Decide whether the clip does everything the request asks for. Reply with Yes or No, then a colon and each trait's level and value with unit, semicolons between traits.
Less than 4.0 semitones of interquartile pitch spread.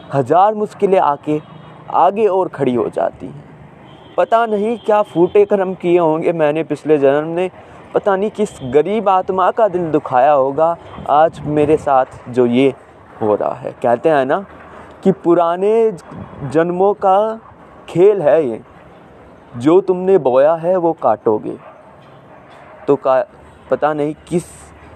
No: average, 4.6 semitones